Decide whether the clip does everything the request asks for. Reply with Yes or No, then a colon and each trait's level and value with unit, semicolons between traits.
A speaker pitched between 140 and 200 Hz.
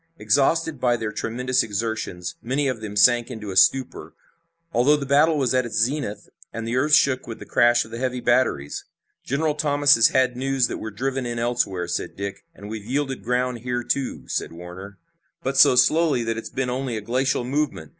No: low, 125 Hz